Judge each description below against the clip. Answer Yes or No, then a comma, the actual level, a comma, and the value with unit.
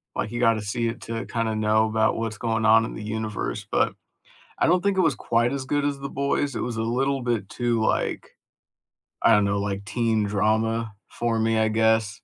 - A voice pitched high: No, low, 115 Hz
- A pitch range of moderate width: No, narrow, 1.8 semitones